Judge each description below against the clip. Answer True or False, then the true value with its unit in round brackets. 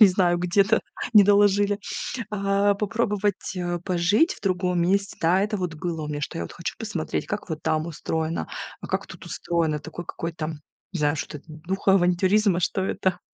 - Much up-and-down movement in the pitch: False (3.3 semitones)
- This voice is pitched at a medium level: True (180 Hz)